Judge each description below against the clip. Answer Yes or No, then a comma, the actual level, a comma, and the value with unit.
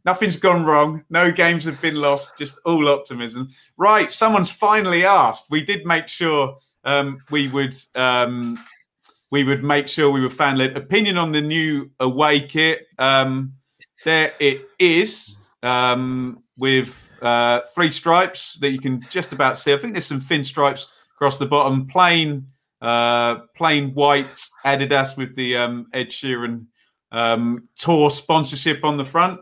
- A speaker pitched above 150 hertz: No, medium, 140 Hz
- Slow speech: No, average, 155 wpm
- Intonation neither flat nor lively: Yes, average, 3.8 semitones